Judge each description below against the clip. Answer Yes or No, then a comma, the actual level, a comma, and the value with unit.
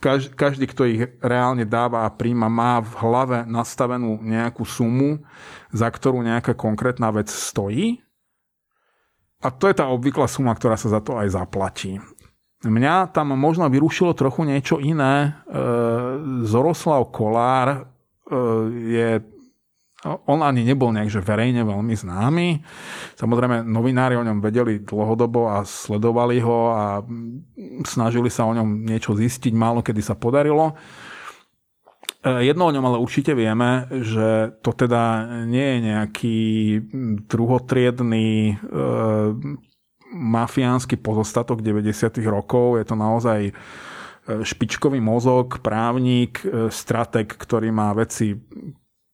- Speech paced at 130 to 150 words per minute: No, average, 115 wpm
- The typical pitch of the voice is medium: No, low, 120 Hz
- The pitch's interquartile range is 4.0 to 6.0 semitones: No, average, 2.7 semitones